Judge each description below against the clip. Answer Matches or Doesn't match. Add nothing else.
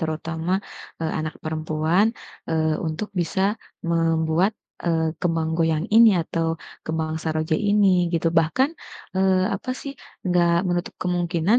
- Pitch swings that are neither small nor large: Doesn't match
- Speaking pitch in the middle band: Matches